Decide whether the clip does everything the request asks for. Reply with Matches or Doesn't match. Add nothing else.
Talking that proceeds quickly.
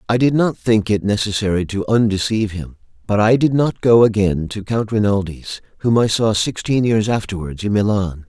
Doesn't match